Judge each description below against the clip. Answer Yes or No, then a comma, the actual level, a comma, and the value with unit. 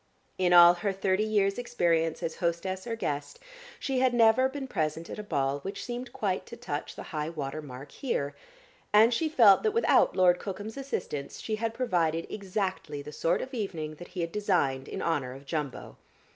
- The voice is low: No, medium, 185 Hz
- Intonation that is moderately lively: No, wide, 6.2 semitones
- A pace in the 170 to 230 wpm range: Yes, average, 190 wpm